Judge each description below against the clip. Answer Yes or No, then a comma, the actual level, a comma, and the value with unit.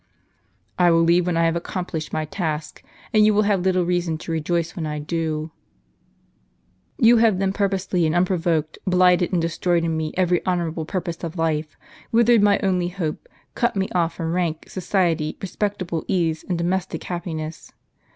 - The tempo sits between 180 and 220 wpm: No, average, 170 wpm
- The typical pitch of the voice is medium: Yes, medium, 175 Hz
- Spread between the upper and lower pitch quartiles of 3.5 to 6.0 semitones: No, narrow, 2.4 semitones